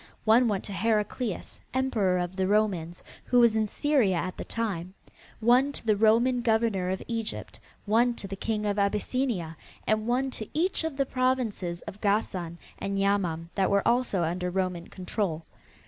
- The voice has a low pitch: No, high, 210 Hz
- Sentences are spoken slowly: No, average, 170 wpm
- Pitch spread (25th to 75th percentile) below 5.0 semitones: Yes, average, 4.1 semitones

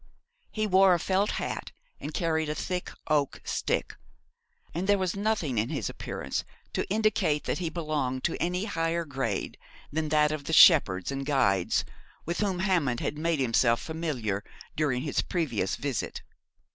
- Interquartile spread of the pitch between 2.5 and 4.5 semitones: No, average, 4.9 semitones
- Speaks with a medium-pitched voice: Yes, medium, 155 Hz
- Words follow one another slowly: No, average, 160 wpm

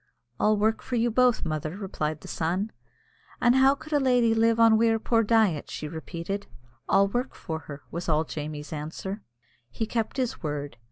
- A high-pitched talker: Yes, high, 205 Hz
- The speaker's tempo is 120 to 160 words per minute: No, average, 180 wpm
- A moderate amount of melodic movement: No, wide, 6.4 semitones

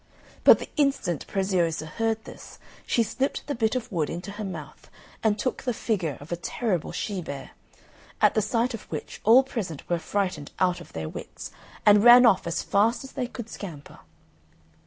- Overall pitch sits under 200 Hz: No, high, 205 Hz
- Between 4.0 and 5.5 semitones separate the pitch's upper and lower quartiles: Yes, average, 5.2 semitones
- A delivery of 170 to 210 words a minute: Yes, average, 185 wpm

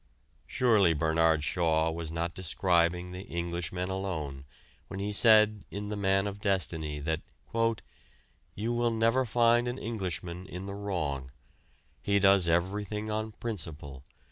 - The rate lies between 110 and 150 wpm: Yes, average, 140 wpm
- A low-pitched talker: Yes, very low, 95 Hz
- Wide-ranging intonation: No, average, 4.1 semitones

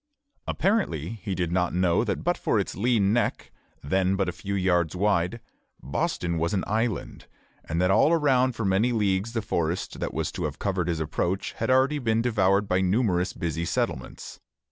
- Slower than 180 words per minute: No, average, 185 wpm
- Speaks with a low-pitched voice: Yes, very low, 95 Hz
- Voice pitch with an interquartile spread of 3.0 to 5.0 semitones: Yes, average, 4.4 semitones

